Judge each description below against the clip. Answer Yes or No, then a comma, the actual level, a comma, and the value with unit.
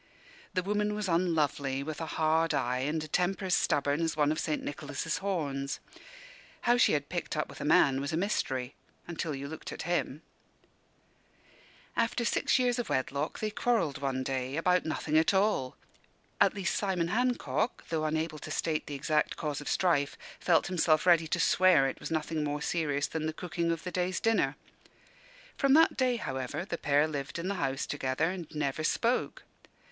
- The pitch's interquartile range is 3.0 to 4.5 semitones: Yes, average, 4.1 semitones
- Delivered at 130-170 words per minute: No, average, 185 wpm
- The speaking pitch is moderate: Yes, medium, 160 Hz